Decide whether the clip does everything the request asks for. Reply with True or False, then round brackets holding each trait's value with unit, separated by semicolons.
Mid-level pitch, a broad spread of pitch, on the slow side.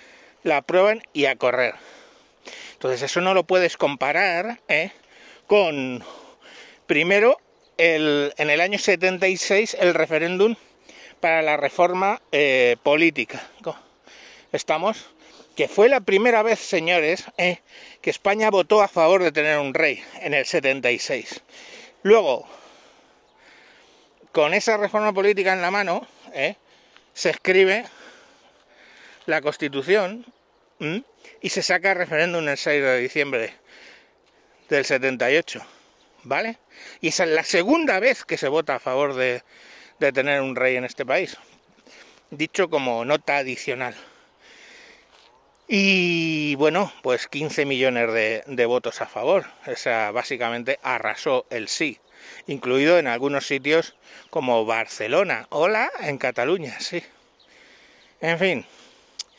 True (175 Hz; 5.9 semitones; 120 wpm)